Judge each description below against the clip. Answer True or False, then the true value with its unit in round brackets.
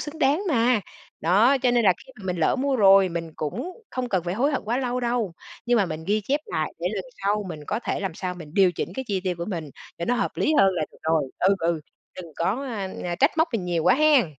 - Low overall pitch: False (200 Hz)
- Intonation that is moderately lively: False (6.3 semitones)